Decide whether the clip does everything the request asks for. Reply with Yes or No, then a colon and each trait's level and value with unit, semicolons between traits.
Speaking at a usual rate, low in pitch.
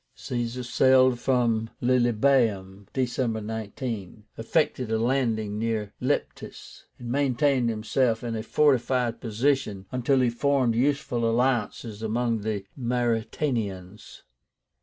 No: slow, 105 wpm; low, 120 Hz